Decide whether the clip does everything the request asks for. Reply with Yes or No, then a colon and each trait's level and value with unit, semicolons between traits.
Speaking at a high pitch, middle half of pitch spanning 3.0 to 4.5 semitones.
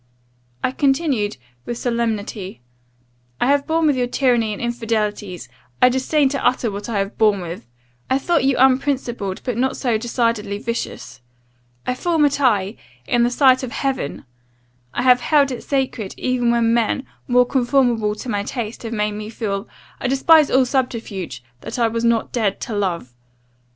Yes: high, 240 Hz; average, 3.7 semitones